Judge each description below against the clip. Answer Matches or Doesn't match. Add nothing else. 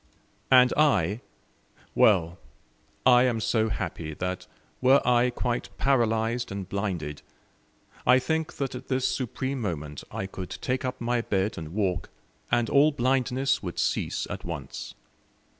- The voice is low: Matches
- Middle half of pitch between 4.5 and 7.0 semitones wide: Matches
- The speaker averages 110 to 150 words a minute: Matches